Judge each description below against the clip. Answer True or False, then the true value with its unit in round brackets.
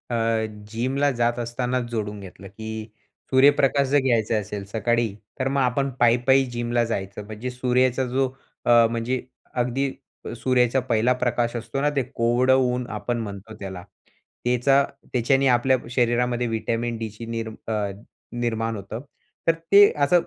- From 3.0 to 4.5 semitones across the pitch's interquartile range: False (2.4 semitones)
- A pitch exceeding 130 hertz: False (120 Hz)